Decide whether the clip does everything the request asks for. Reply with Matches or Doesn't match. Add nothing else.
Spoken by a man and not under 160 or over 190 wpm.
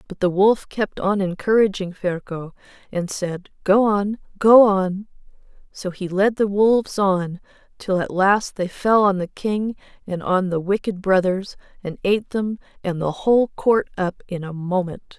Doesn't match